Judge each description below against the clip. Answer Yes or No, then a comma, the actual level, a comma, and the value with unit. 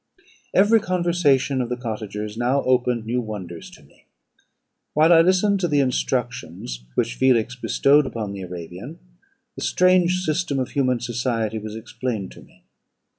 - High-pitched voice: No, low, 125 Hz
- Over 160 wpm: No, average, 150 wpm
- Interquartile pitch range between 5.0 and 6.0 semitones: Yes, wide, 5.5 semitones